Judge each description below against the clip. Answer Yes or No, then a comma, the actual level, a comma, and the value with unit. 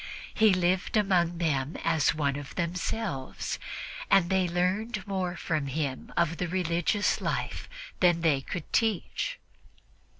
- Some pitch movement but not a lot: Yes, average, 3.0 semitones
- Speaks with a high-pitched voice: No, medium, 175 Hz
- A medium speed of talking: No, slow, 130 wpm